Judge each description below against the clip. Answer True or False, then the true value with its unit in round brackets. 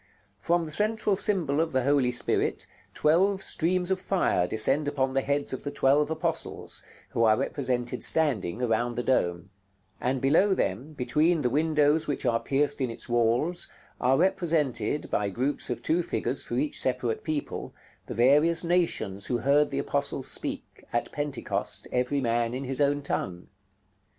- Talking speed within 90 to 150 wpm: False (165 wpm)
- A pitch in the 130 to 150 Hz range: True (140 Hz)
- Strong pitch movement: False (4.3 semitones)